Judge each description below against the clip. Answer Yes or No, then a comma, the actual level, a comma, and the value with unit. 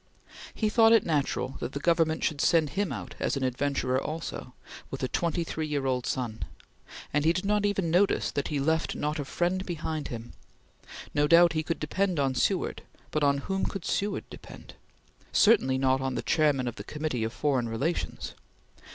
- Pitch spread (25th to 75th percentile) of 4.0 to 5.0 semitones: Yes, average, 4.4 semitones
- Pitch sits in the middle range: Yes, medium, 150 Hz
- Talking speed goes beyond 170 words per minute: Yes, average, 190 wpm